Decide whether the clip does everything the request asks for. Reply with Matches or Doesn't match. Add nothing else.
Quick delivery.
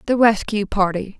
Doesn't match